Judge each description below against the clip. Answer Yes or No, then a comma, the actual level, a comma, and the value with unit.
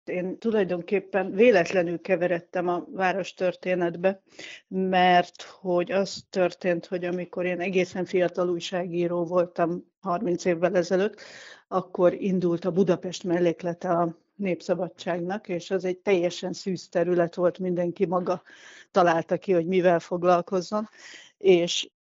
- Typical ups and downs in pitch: No, narrow, 1.2 semitones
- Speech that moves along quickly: No, average, 115 wpm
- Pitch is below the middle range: No, medium, 180 Hz